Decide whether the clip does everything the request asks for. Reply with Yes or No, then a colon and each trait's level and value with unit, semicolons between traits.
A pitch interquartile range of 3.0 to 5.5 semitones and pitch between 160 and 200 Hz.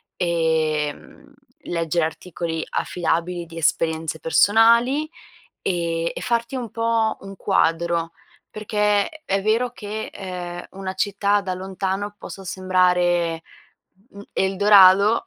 Yes: average, 3.5 semitones; medium, 185 Hz